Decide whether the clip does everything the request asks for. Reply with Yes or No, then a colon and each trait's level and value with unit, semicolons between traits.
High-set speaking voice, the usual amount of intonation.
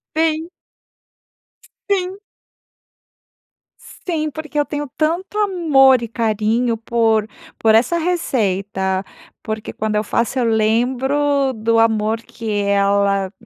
No: high, 235 Hz; wide, 5.9 semitones